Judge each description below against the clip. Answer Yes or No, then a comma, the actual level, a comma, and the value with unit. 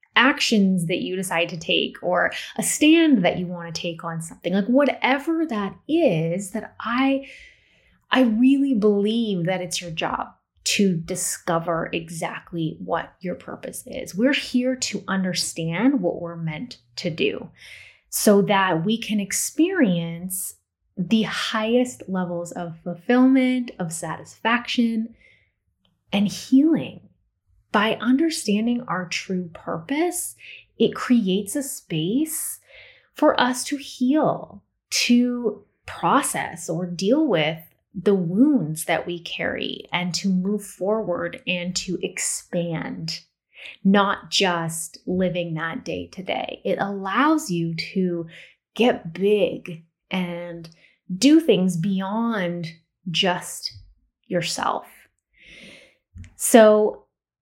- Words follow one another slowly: Yes, slow, 115 wpm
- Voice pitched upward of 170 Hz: Yes, high, 190 Hz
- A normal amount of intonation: No, wide, 6.1 semitones